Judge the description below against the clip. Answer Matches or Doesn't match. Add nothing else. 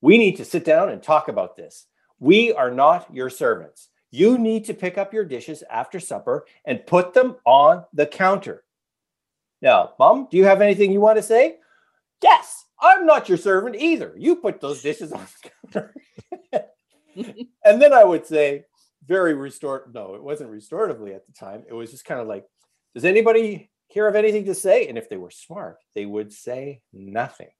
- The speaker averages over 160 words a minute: Matches